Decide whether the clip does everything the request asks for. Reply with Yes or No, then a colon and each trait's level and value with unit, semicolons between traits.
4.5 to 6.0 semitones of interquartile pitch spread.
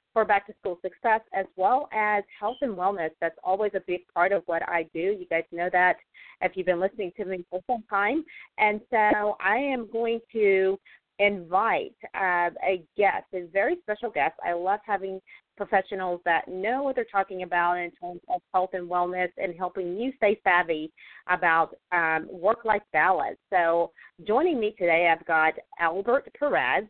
No: average, 3.3 semitones